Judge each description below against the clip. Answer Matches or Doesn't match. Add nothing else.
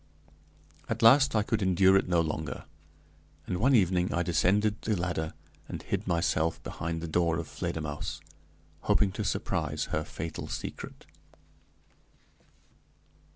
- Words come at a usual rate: Doesn't match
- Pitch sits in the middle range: Doesn't match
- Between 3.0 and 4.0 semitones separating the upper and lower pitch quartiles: Matches